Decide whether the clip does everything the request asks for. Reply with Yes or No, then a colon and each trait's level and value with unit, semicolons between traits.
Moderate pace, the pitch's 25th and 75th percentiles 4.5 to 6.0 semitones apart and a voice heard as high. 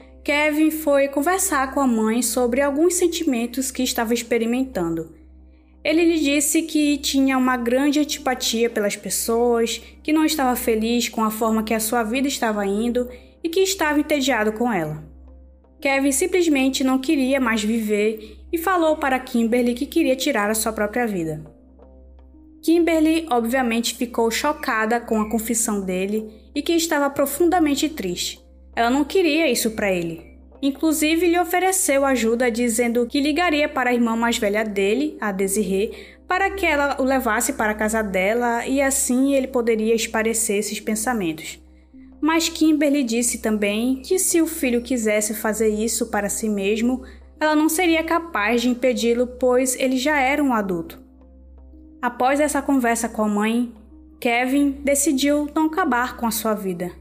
Yes: average, 155 wpm; average, 4.9 semitones; high, 245 Hz